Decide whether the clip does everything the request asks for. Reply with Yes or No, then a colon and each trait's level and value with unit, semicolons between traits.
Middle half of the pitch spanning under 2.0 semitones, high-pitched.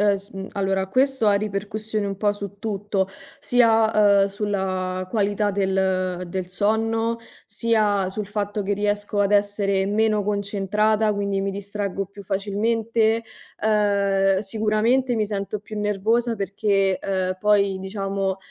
Yes: narrow, 1.6 semitones; high, 205 Hz